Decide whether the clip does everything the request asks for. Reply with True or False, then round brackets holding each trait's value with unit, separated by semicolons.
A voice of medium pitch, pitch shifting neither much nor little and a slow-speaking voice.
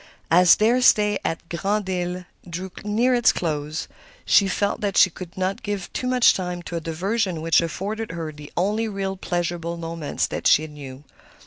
False (180 Hz; 3.8 semitones; 180 wpm)